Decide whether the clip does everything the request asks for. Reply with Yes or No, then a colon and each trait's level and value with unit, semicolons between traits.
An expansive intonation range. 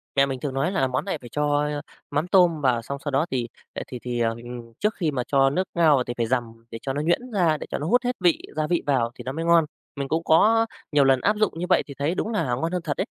No: average, 4.8 semitones